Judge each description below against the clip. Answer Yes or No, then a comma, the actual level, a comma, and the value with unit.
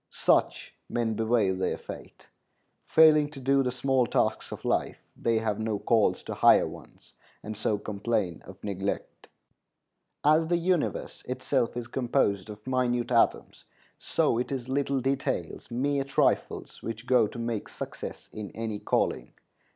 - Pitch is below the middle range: Yes, low, 120 Hz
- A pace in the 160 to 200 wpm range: No, average, 150 wpm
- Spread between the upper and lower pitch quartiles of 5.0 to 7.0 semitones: No, average, 3.8 semitones